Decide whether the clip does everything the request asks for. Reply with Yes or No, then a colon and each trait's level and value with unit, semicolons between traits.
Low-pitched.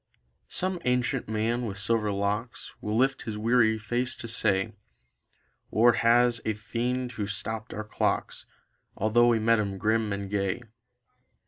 Yes: low, 110 Hz